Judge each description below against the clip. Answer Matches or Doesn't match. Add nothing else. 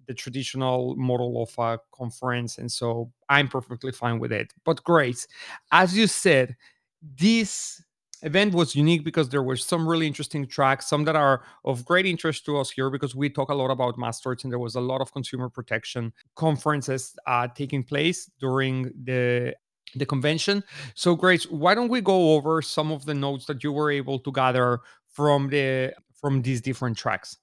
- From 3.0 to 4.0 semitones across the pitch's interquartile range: Matches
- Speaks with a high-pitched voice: Doesn't match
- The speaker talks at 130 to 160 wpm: Doesn't match